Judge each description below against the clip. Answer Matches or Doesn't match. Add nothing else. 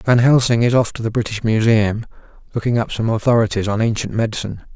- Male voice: Matches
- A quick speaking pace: Doesn't match